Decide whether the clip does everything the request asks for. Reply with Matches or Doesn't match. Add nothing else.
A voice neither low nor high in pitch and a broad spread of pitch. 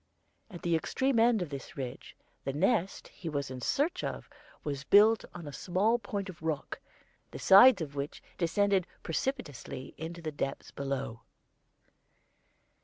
Matches